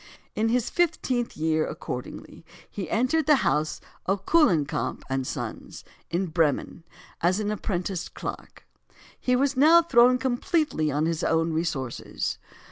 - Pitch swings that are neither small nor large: No, wide, 8.0 semitones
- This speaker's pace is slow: Yes, slow, 130 wpm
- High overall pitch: Yes, high, 195 Hz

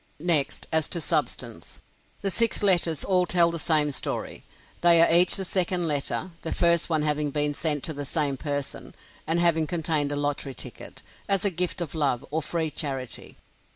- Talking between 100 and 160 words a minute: No, average, 185 wpm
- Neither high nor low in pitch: Yes, medium, 160 Hz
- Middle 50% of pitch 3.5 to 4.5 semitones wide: No, average, 2.9 semitones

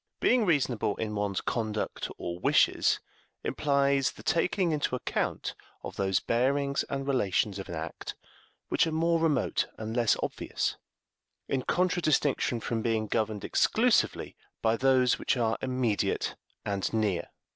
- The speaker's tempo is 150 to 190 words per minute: No, slow, 135 wpm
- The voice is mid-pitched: No, low, 120 Hz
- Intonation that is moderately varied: Yes, average, 4.6 semitones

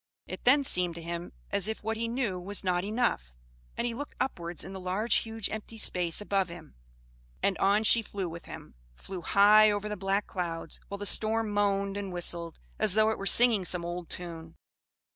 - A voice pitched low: No, high, 195 Hz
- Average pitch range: Yes, average, 3.4 semitones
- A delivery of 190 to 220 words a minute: Yes, average, 200 wpm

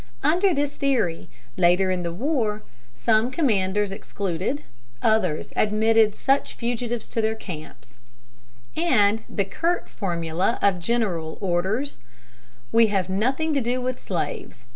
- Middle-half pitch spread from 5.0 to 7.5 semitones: Yes, average, 5.3 semitones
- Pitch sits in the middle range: No, high, 215 Hz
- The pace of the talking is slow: Yes, slow, 125 wpm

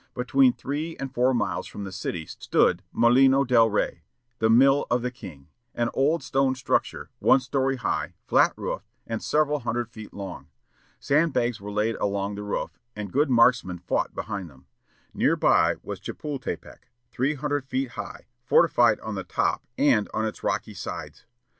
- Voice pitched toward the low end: Yes, low, 120 Hz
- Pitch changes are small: No, average, 4.3 semitones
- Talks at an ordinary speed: Yes, average, 165 wpm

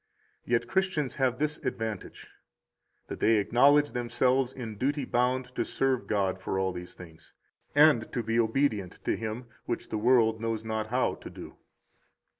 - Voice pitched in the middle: No, low, 120 Hz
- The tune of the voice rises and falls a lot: No, average, 3.1 semitones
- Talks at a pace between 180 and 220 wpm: No, average, 160 wpm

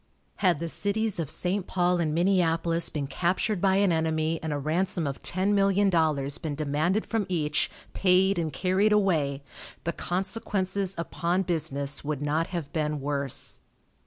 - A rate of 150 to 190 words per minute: Yes, average, 160 wpm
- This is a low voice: No, medium, 170 Hz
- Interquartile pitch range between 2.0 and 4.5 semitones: Yes, average, 3.9 semitones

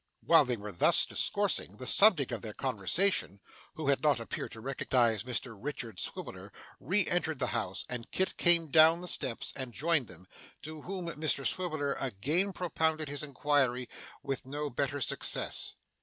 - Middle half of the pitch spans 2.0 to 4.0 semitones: No, average, 4.9 semitones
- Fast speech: No, average, 165 wpm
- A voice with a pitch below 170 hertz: Yes, medium, 140 Hz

